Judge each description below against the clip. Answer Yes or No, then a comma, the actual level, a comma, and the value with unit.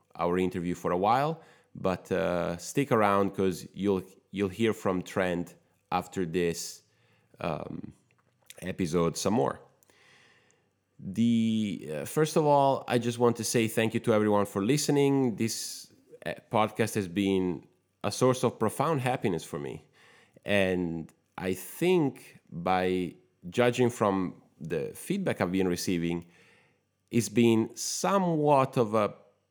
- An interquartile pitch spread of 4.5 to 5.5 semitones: Yes, average, 4.8 semitones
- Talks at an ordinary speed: No, slow, 130 wpm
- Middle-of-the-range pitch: No, low, 105 Hz